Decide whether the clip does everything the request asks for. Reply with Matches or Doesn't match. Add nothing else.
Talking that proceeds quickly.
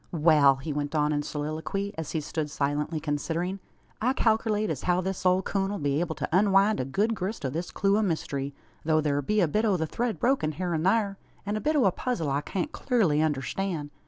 Matches